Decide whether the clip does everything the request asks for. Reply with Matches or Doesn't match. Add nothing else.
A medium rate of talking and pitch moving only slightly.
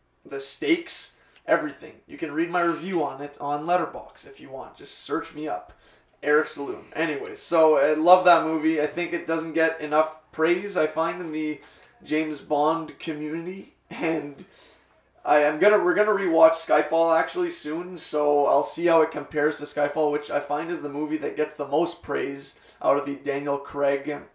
Matches